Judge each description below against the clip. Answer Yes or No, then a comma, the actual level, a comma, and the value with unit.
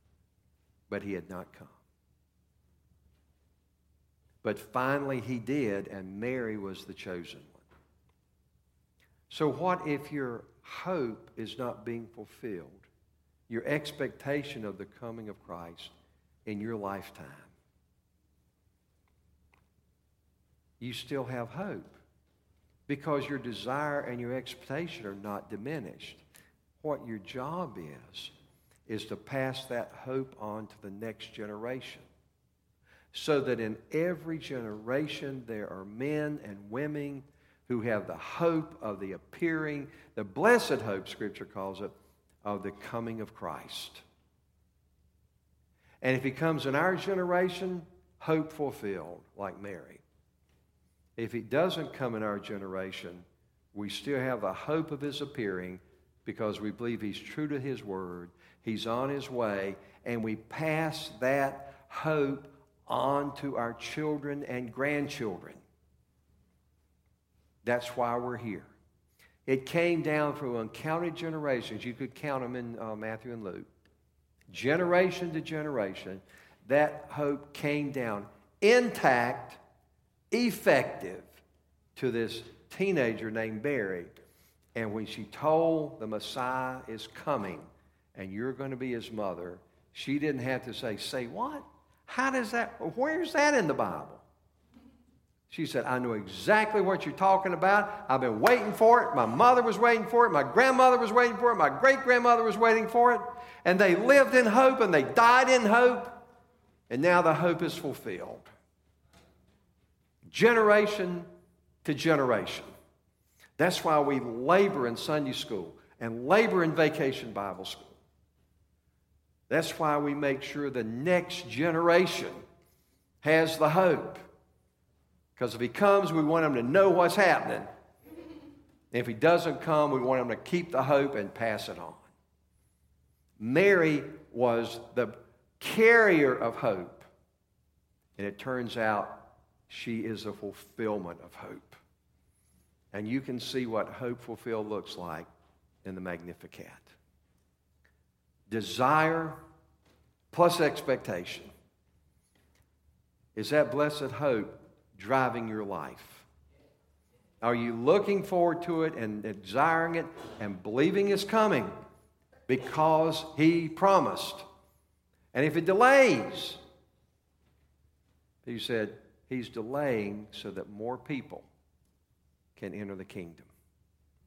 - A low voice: Yes, low, 120 Hz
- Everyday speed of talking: No, slow, 130 wpm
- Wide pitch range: Yes, wide, 8.6 semitones